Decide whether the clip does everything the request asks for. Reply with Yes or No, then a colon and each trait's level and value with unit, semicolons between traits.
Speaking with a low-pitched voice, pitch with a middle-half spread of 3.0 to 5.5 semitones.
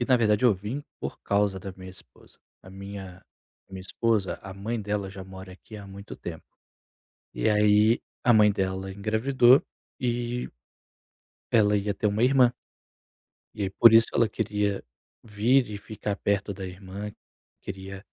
No: low, 105 Hz; narrow, 2.6 semitones